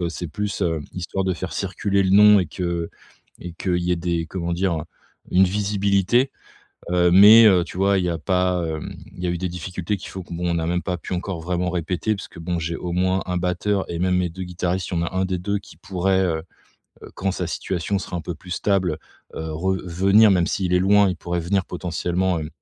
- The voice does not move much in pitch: Yes, narrow, 1.8 semitones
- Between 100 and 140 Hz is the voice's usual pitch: No, very low, 90 Hz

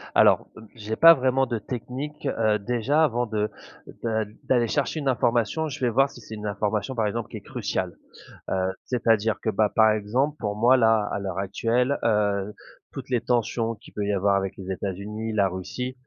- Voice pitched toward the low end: Yes, low, 110 Hz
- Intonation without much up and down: No, average, 3.3 semitones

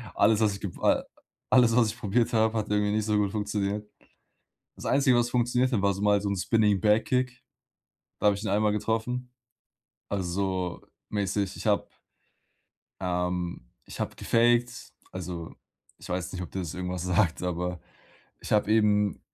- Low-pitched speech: Yes, low, 105 Hz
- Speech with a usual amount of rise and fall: Yes, average, 3.4 semitones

